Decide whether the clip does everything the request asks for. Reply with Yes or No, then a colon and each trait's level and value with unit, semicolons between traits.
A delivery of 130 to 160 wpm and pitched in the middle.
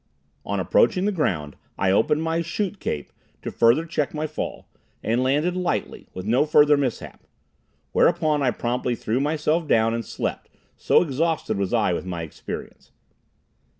Yes: average, 155 wpm; medium, 145 Hz